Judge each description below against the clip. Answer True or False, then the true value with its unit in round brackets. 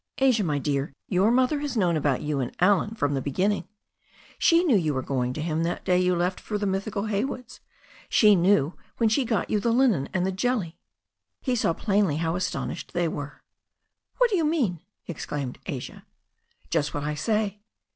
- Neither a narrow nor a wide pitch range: False (6.4 semitones)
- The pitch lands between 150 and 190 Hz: True (185 Hz)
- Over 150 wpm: True (190 wpm)